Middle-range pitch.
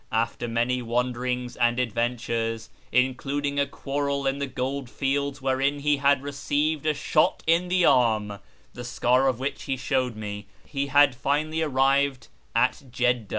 No: low, 130 Hz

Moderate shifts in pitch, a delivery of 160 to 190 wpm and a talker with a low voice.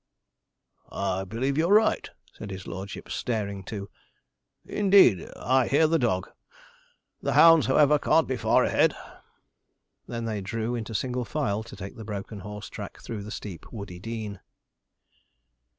No: average, 4.6 semitones; average, 145 wpm; low, 110 Hz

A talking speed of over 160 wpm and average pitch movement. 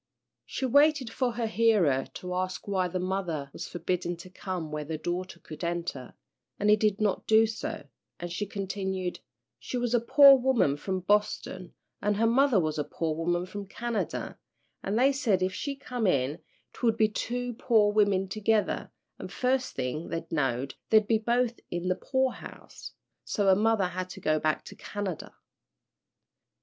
Yes: average, 175 wpm; average, 4.6 semitones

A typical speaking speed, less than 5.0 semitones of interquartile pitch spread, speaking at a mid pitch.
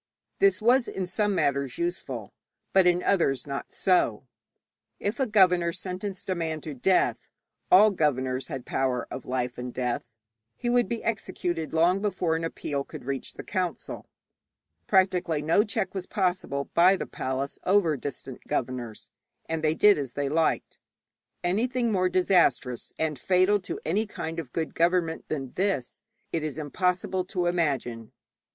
No: average, 155 wpm; wide, 5.4 semitones; medium, 170 Hz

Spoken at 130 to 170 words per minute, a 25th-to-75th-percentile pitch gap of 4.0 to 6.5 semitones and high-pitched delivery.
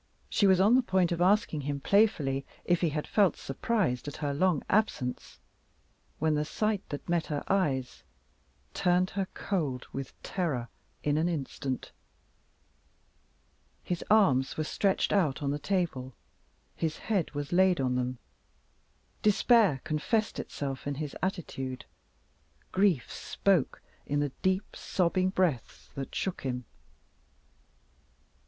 No: slow, 135 wpm; wide, 5.5 semitones; medium, 160 Hz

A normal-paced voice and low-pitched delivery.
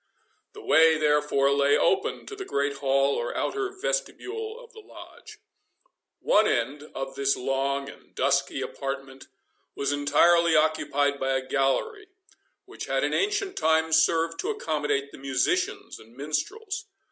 No: average, 145 wpm; medium, 150 Hz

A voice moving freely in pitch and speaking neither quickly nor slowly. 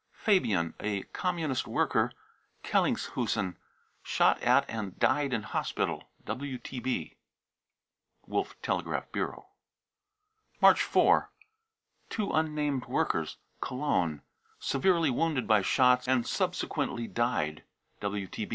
No: wide, 6.2 semitones; slow, 80 wpm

